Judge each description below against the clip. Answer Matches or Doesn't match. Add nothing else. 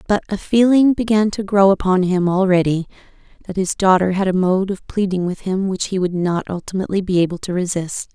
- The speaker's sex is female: Matches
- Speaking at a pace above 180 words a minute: Matches